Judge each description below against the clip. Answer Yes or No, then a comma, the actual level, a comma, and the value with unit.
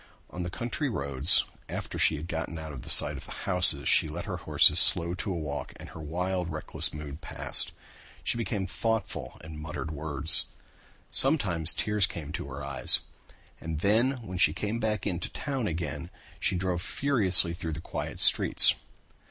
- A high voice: No, very low, 85 Hz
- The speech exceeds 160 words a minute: Yes, average, 175 wpm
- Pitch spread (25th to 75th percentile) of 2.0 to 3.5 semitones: No, average, 4.6 semitones